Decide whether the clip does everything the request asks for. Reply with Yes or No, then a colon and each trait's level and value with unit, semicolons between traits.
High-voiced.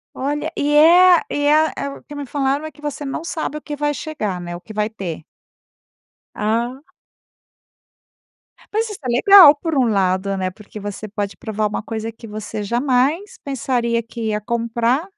Yes: high, 245 Hz